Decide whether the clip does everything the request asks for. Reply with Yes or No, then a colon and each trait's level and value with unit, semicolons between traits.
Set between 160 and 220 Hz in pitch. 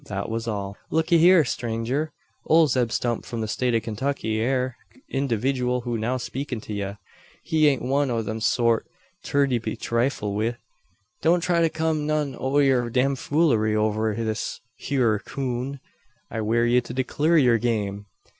No: low, 125 Hz